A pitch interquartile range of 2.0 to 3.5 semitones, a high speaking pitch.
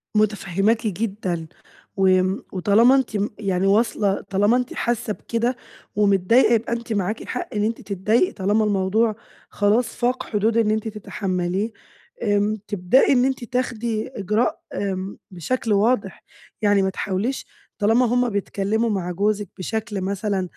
Yes: average, 2.9 semitones; high, 210 Hz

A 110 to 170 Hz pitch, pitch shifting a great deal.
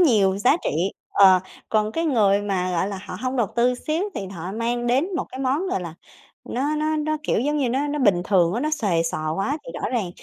No: high, 235 Hz; wide, 7.0 semitones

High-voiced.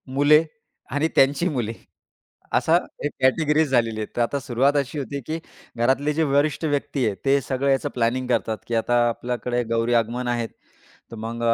No: low, 130 Hz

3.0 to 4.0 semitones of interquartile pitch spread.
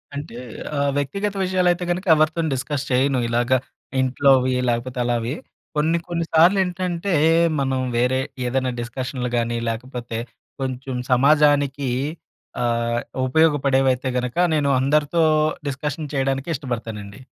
Yes: average, 3.4 semitones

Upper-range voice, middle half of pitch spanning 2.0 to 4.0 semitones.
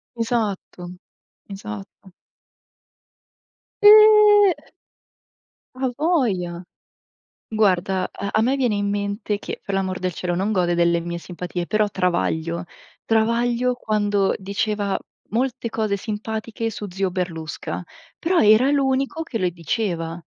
No: high, 205 Hz; average, 4.6 semitones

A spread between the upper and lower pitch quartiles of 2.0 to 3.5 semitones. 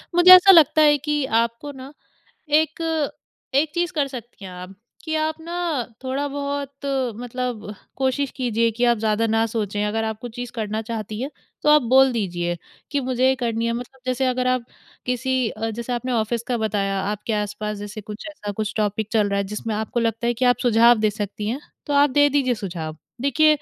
No: average, 4.5 semitones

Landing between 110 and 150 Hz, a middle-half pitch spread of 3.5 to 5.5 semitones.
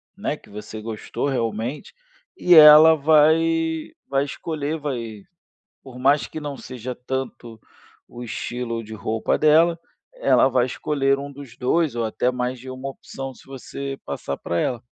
Yes: low, 135 Hz; average, 3.9 semitones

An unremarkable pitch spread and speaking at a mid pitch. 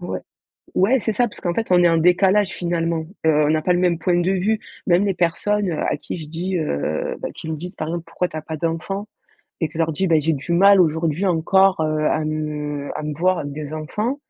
Yes: average, 3.2 semitones; medium, 170 Hz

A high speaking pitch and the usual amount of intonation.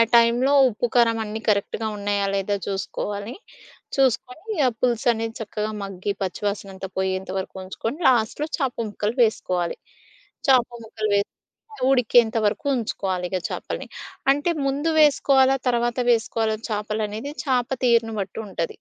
Yes: high, 220 Hz; average, 3.4 semitones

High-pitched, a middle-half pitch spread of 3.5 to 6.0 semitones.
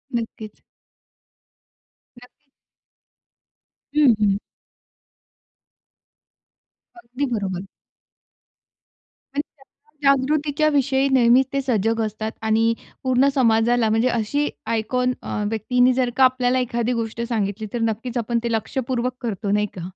No: high, 240 Hz; average, 2.9 semitones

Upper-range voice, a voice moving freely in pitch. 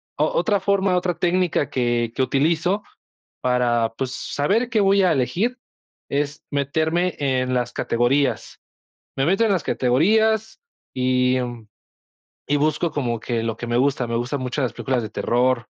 No: medium, 140 Hz; wide, 6.4 semitones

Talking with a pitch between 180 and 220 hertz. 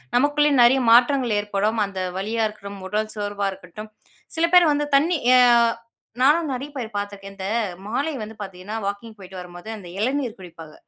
Yes: high, 215 Hz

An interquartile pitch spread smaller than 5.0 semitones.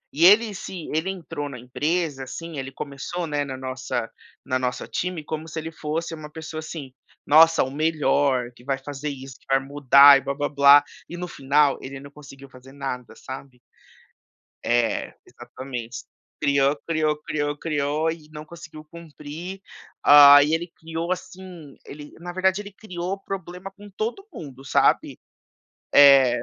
Yes: average, 3.3 semitones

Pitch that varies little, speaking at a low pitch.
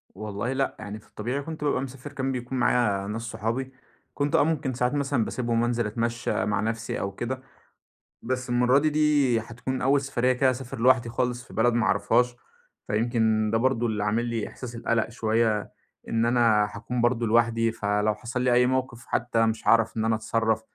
Yes: narrow, 2.3 semitones; low, 120 Hz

